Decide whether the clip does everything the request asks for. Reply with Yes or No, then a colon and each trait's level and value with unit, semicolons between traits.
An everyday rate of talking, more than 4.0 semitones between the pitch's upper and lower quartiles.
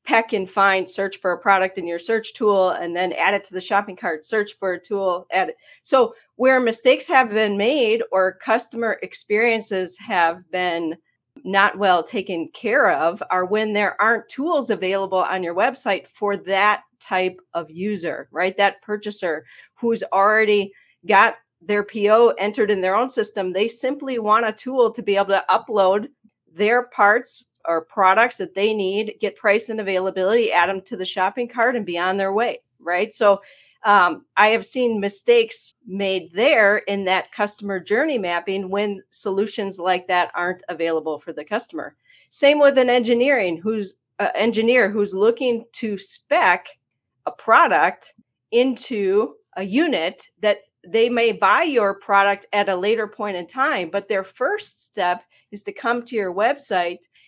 No: average, 170 wpm; average, 3.3 semitones